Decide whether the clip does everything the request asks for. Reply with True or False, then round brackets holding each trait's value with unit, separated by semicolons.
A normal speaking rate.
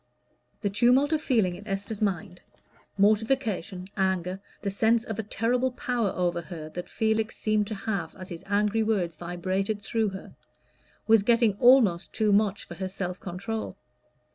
True (160 wpm)